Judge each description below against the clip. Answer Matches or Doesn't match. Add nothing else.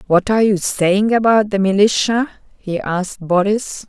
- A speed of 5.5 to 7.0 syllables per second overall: Doesn't match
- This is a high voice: Matches